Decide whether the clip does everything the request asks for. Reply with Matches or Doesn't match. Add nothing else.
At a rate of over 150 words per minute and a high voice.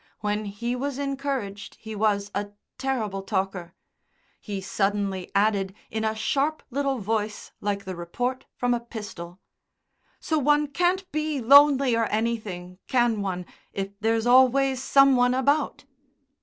Doesn't match